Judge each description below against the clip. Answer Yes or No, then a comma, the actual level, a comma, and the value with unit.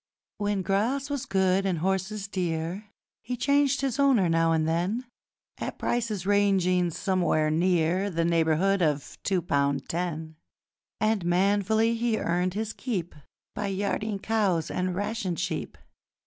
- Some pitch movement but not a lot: Yes, average, 3.9 semitones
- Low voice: No, high, 190 Hz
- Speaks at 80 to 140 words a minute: Yes, slow, 135 wpm